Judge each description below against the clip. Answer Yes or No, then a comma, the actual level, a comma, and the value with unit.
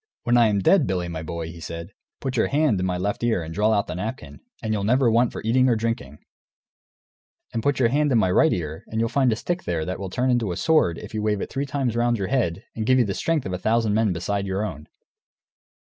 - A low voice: Yes, low, 110 Hz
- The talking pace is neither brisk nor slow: No, fast, 265 wpm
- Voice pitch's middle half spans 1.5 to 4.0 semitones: No, average, 5.1 semitones